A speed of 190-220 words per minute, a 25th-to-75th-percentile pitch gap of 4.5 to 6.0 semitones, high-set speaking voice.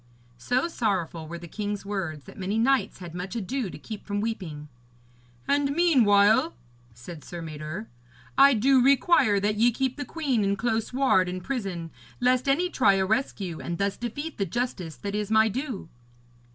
No: average, 175 wpm; wide, 5.6 semitones; high, 210 Hz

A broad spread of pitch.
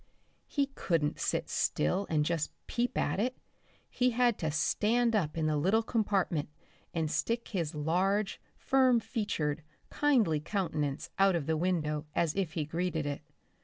Yes: wide, 6.3 semitones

